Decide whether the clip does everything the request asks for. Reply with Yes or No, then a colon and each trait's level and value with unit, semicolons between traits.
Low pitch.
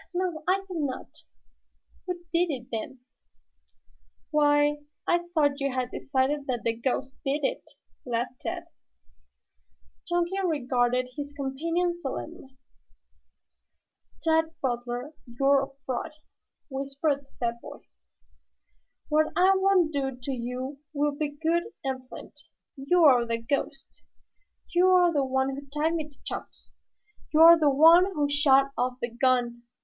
No: very high, 280 Hz